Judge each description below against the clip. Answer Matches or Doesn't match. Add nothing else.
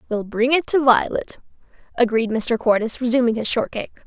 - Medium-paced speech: Matches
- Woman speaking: Matches